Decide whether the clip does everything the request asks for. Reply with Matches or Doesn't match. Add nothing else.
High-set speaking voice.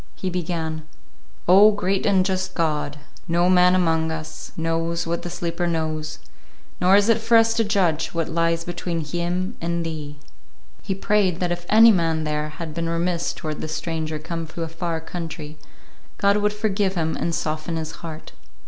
Doesn't match